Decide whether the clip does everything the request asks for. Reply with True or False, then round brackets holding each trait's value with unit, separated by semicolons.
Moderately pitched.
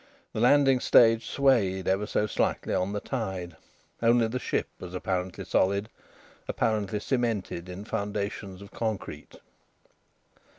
False (105 Hz)